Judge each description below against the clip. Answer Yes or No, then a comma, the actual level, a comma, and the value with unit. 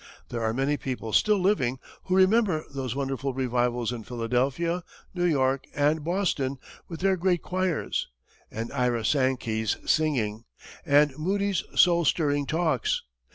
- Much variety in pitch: Yes, wide, 5.7 semitones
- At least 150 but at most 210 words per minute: No, slow, 135 wpm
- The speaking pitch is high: No, medium, 140 Hz